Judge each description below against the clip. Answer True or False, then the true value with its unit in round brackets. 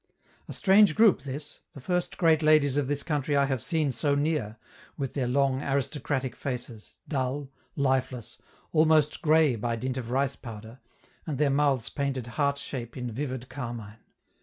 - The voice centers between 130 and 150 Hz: True (140 Hz)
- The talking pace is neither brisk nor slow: True (160 wpm)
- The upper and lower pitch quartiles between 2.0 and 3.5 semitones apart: True (2.8 semitones)